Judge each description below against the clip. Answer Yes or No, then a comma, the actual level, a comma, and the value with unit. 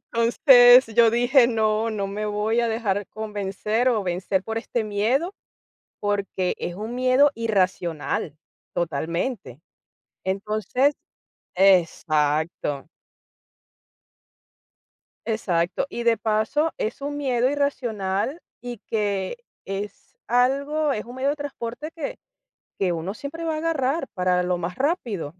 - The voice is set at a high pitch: Yes, high, 220 Hz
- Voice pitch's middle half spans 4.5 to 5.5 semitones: Yes, average, 5.2 semitones